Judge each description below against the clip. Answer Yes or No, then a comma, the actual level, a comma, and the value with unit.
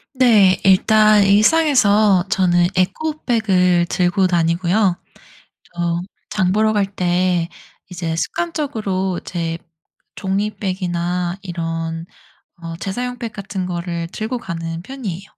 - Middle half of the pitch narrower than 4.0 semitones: Yes, average, 3.5 semitones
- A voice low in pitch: No, medium, 185 Hz